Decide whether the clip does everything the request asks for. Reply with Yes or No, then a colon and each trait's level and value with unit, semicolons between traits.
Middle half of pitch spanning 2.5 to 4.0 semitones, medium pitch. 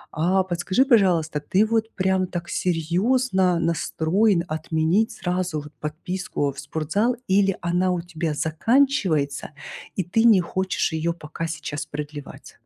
Yes: average, 3.4 semitones; medium, 175 Hz